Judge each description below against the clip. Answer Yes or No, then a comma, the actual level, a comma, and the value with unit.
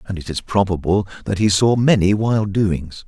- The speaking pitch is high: No, low, 100 Hz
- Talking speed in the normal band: Yes, average, 195 wpm